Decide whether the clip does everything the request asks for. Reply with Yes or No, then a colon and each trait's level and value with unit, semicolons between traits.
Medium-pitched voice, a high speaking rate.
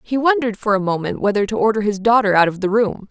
No: high, 210 Hz; fast, 270 wpm